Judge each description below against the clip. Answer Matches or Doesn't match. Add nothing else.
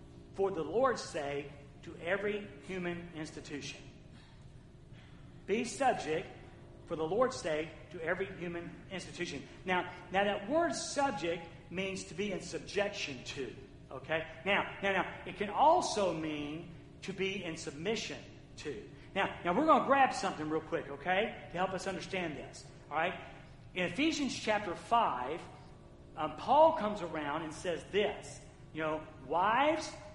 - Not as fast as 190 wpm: Matches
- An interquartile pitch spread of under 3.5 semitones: Doesn't match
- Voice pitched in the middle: Matches